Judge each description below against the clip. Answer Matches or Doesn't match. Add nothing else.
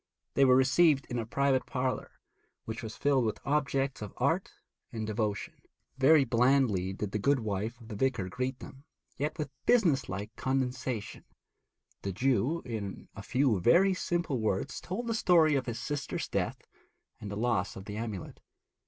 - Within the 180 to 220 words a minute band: Doesn't match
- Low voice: Matches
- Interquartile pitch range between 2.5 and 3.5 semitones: Doesn't match